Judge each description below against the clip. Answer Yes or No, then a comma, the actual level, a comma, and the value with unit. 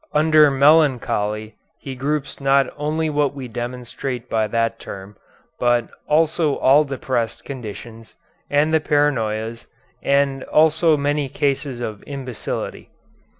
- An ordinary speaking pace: No, slow, 115 wpm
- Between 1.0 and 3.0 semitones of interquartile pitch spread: No, average, 3.8 semitones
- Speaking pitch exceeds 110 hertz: Yes, low, 135 Hz